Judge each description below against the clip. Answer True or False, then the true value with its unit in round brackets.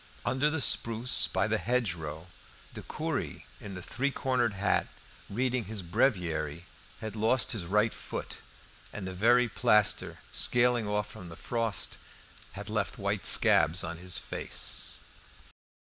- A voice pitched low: True (105 Hz)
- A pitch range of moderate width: True (4.7 semitones)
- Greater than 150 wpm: False (140 wpm)